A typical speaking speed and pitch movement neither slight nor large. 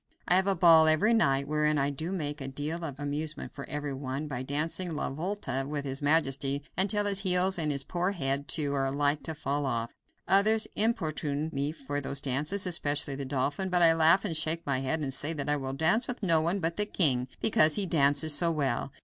No: fast, 225 wpm; average, 3.7 semitones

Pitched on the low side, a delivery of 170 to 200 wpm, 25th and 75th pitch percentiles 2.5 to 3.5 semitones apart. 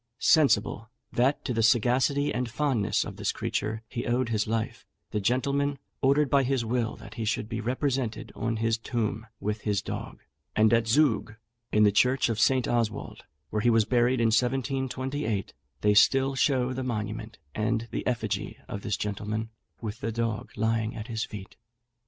Yes: low, 115 Hz; average, 175 wpm; average, 3.0 semitones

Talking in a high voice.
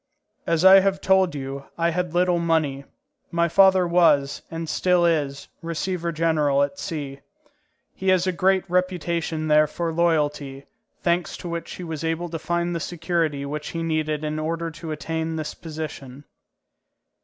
No: medium, 165 Hz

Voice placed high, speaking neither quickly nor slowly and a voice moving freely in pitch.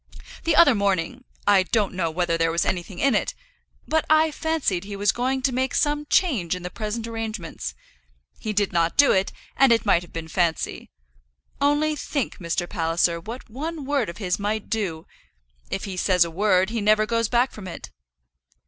Yes: high, 210 Hz; average, 190 wpm; wide, 6.4 semitones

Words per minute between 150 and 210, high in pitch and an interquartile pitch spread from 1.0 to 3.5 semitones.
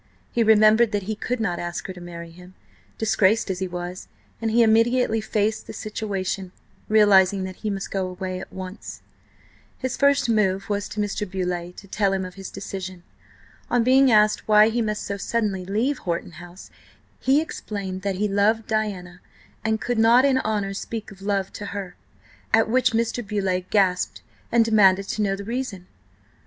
Yes: average, 180 wpm; high, 205 Hz; average, 2.9 semitones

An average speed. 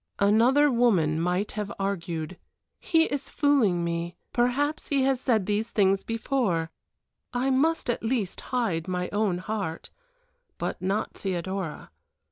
No: slow, 130 wpm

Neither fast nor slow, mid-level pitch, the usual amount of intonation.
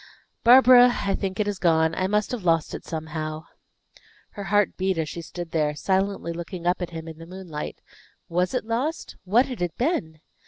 Yes: average, 195 wpm; medium, 180 Hz; average, 4.1 semitones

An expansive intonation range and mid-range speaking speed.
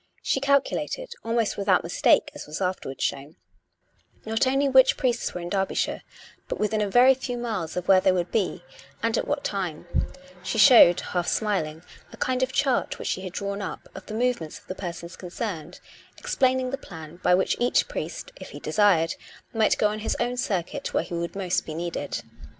Yes: wide, 5.8 semitones; average, 195 wpm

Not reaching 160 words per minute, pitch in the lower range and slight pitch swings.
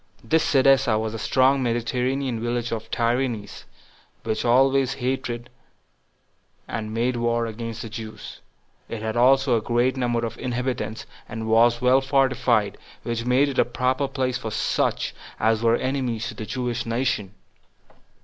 Yes: average, 150 wpm; low, 120 Hz; narrow, 2.3 semitones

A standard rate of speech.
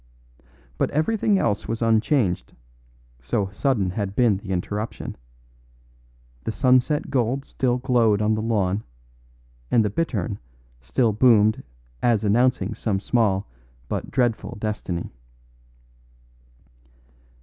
No: slow, 105 wpm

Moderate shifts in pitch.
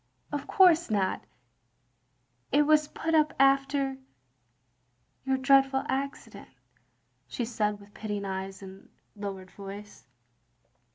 No: wide, 6.0 semitones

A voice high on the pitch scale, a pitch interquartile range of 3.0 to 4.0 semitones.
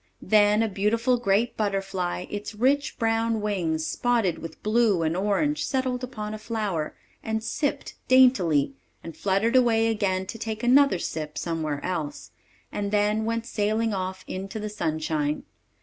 Yes: high, 210 Hz; average, 3.7 semitones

